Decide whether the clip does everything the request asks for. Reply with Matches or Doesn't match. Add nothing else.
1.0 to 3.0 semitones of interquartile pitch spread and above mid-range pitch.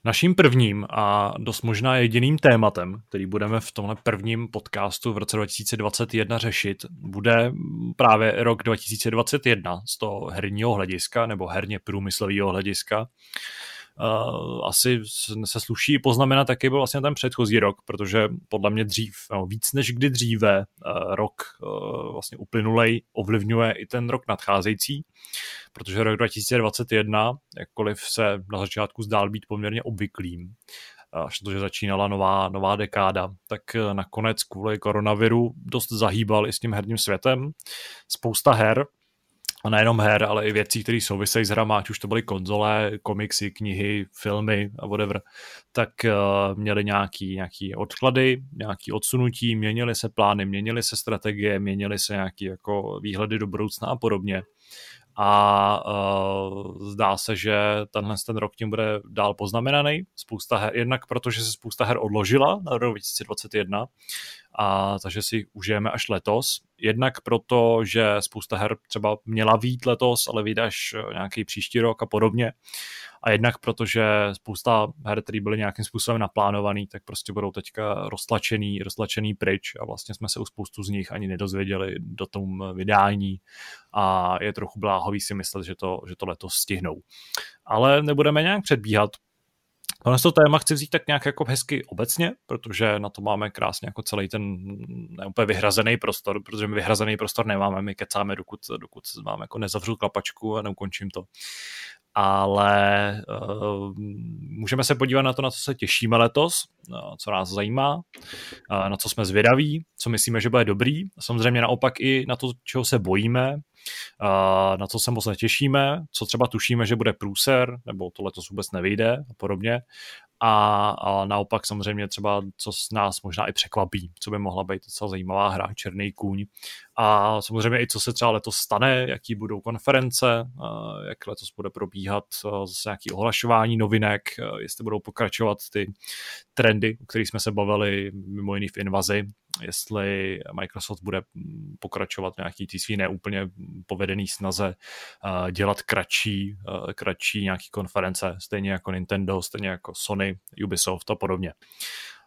Doesn't match